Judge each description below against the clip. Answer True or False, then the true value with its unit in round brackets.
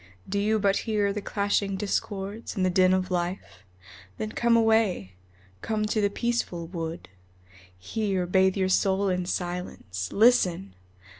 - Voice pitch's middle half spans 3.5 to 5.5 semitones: False (2.8 semitones)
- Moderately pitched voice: False (195 Hz)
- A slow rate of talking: False (145 wpm)